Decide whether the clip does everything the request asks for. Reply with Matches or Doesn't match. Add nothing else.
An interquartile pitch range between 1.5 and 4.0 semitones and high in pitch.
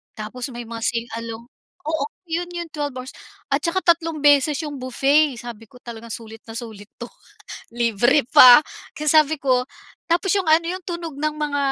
Doesn't match